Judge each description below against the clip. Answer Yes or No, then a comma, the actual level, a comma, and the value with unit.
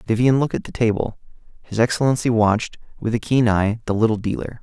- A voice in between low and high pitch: No, low, 115 Hz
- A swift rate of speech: No, average, 195 wpm